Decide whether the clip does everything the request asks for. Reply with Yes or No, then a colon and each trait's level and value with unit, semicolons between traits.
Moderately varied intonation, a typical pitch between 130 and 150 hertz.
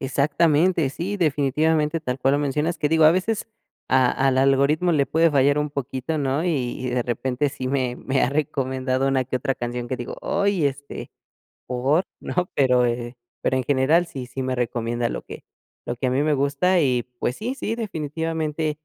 Yes: average, 3.5 semitones; medium, 140 Hz